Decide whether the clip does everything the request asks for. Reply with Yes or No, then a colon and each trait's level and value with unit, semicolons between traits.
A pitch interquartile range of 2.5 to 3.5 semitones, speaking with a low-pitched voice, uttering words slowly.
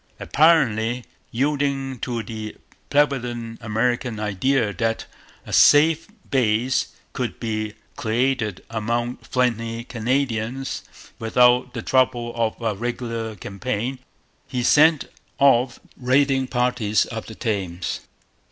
Yes: average, 2.9 semitones; low, 120 Hz; slow, 105 wpm